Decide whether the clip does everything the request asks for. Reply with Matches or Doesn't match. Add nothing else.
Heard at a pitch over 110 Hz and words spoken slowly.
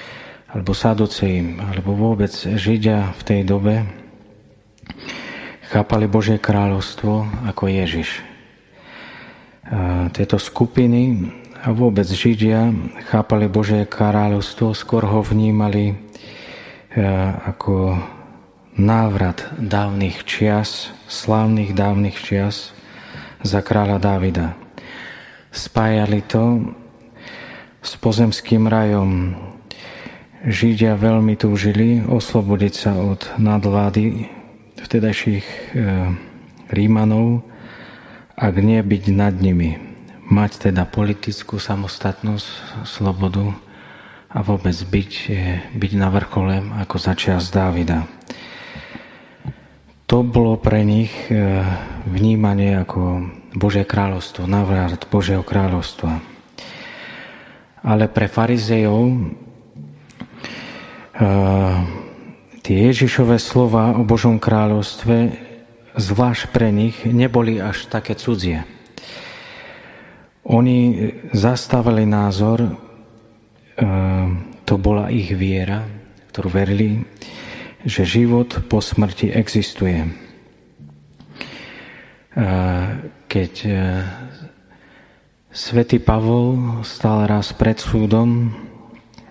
Doesn't match